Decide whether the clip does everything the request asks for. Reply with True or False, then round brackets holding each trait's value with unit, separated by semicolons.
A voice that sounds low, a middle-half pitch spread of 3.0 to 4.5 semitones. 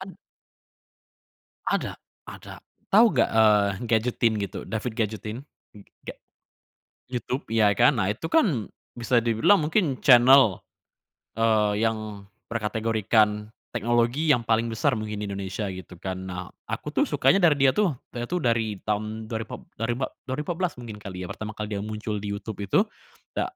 False (110 Hz; 2.6 semitones)